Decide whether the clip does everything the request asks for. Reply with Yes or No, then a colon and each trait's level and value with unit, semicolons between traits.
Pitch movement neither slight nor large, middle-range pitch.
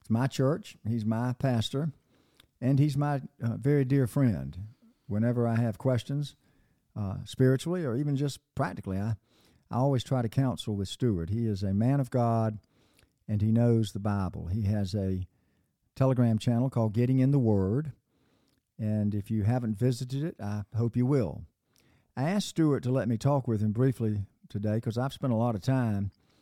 No: average, 3.7 semitones; low, 120 Hz